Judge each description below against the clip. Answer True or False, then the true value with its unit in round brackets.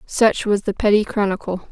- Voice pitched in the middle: False (205 Hz)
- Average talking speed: True (175 wpm)